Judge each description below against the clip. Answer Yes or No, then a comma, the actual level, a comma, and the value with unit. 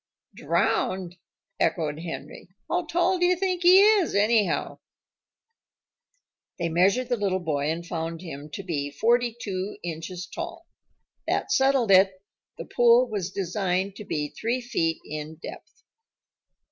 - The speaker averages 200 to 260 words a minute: No, slow, 135 wpm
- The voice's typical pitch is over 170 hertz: Yes, high, 190 Hz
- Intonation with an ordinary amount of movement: No, wide, 6.5 semitones